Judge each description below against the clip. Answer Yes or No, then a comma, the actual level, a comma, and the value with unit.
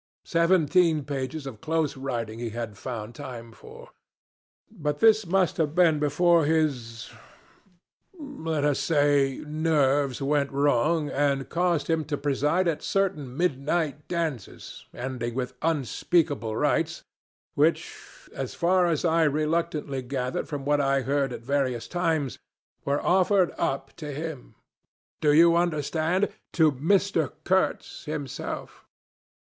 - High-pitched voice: No, medium, 150 Hz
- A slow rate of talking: Yes, slow, 125 wpm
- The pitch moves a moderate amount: Yes, average, 3.5 semitones